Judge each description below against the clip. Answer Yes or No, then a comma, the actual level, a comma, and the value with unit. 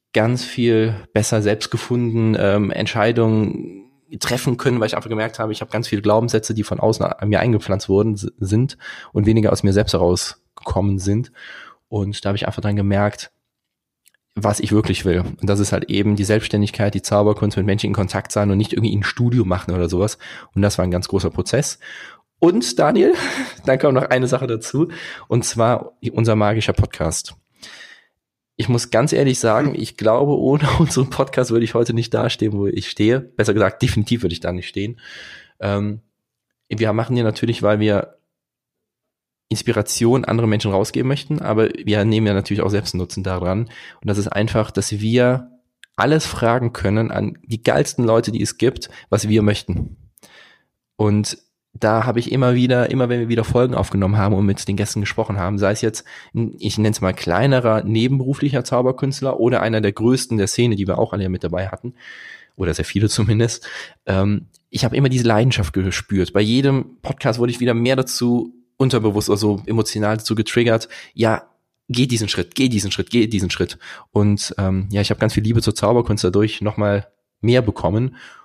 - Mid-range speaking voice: No, low, 110 Hz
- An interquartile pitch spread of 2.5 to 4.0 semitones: Yes, average, 2.9 semitones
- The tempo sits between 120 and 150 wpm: No, average, 185 wpm